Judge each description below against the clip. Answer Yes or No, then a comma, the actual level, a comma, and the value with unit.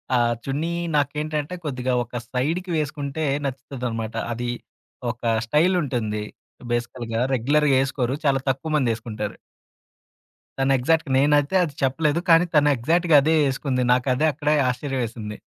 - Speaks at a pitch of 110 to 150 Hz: Yes, low, 135 Hz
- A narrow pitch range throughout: No, average, 3.6 semitones